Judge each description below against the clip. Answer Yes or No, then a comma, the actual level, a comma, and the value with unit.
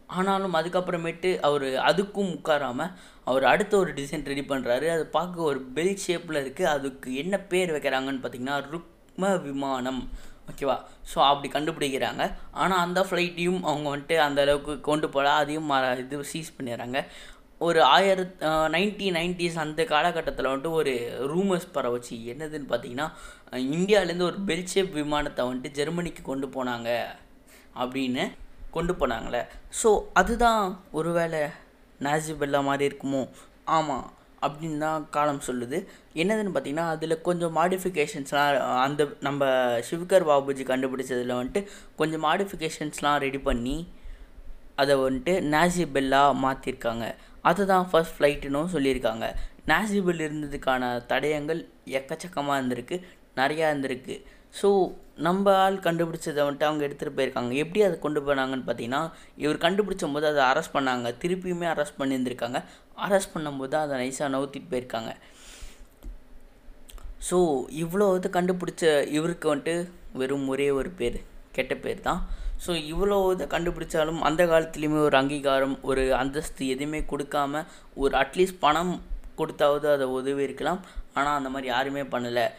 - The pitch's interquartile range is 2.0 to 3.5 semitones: No, average, 4.1 semitones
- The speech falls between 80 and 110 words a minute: No, average, 125 wpm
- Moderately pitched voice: Yes, medium, 150 Hz